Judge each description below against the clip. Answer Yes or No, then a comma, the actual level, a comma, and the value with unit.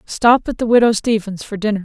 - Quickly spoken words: Yes, fast, 230 wpm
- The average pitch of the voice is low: No, high, 220 Hz